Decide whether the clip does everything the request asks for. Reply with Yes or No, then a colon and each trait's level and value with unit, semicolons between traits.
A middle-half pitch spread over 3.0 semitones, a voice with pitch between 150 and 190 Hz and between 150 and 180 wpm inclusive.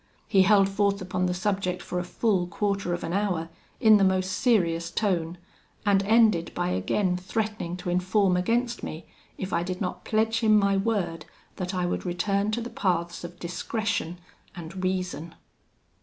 No: average, 2.7 semitones; medium, 185 Hz; average, 170 wpm